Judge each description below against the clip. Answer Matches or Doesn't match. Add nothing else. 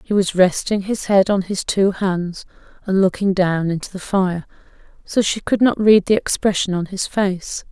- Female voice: Matches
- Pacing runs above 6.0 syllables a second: Doesn't match